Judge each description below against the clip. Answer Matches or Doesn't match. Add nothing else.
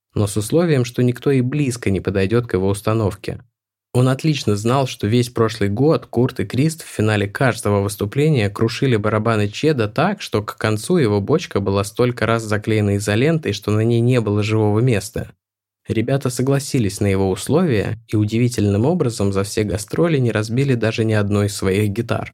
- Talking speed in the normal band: Doesn't match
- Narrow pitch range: Doesn't match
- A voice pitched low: Matches